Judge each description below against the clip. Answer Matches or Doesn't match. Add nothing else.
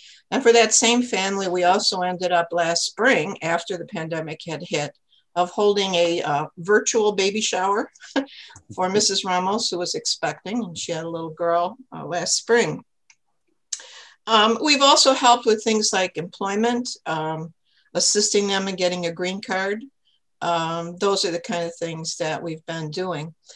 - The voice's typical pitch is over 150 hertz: Matches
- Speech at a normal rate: Matches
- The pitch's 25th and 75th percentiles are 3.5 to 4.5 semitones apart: Matches